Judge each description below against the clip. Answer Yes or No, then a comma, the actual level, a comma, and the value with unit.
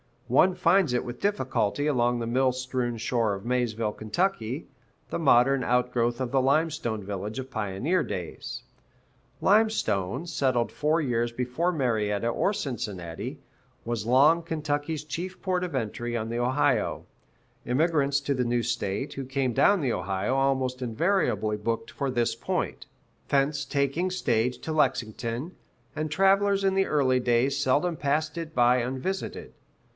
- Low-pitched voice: Yes, low, 130 Hz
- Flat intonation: No, average, 4.6 semitones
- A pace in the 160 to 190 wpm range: No, average, 145 wpm